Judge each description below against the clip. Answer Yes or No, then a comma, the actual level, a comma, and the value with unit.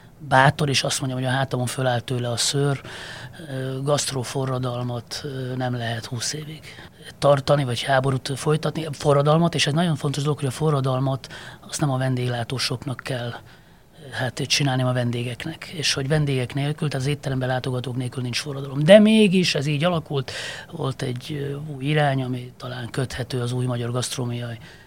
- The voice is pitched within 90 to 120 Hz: No, low, 135 Hz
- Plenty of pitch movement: No, average, 2.7 semitones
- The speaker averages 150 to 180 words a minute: Yes, fast, 155 wpm